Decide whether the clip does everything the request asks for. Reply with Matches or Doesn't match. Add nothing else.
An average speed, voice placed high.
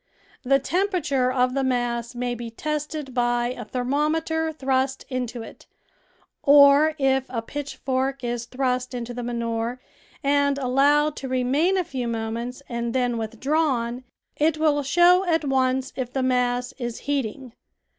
Matches